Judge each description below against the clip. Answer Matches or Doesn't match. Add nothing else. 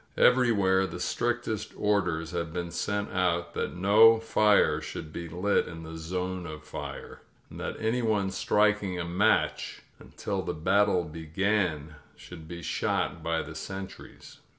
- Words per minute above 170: Doesn't match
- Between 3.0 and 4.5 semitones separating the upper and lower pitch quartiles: Matches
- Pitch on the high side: Doesn't match